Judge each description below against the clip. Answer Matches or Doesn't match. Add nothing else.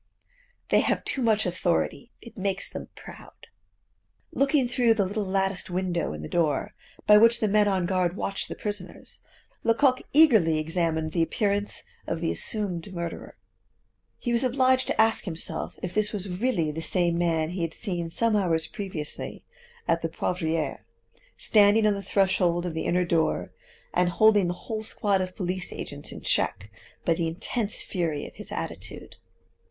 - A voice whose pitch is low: Doesn't match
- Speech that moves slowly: Doesn't match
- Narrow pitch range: Doesn't match